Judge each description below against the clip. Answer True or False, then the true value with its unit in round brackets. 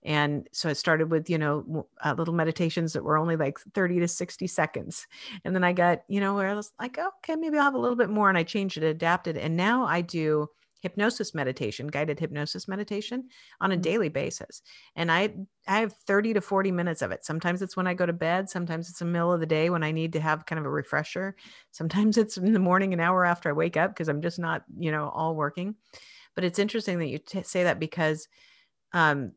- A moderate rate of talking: False (240 wpm)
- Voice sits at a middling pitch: True (175 Hz)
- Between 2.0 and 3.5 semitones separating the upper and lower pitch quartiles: False (3.9 semitones)